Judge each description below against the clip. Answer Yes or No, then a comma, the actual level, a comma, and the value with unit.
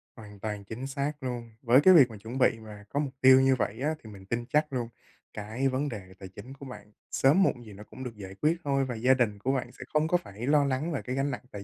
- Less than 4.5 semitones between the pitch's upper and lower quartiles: Yes, average, 4.0 semitones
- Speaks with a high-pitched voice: No, low, 125 Hz